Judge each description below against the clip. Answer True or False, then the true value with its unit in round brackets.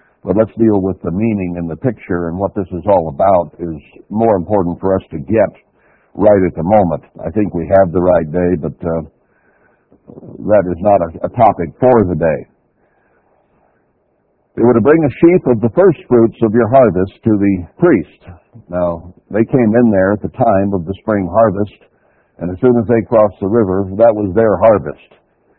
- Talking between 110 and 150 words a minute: False (195 wpm)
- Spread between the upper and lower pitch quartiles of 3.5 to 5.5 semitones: True (4.2 semitones)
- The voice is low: True (100 Hz)